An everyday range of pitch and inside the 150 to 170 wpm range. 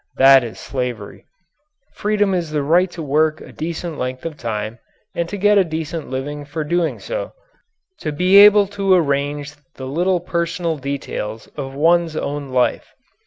Yes: average, 4.2 semitones; average, 165 wpm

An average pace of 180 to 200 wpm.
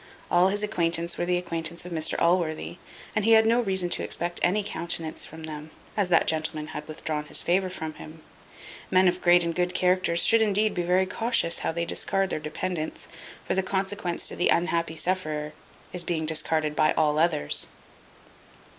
Yes: average, 185 wpm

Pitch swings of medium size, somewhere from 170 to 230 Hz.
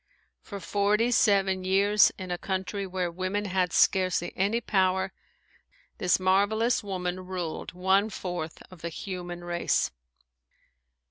No: narrow, 1.8 semitones; high, 190 Hz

